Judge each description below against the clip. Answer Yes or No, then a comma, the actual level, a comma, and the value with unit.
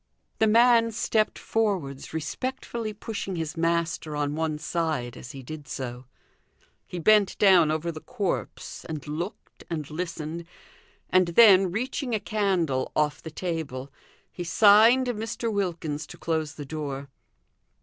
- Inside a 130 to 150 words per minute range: Yes, average, 140 wpm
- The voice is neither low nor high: Yes, medium, 170 Hz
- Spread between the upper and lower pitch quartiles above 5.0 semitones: Yes, wide, 5.5 semitones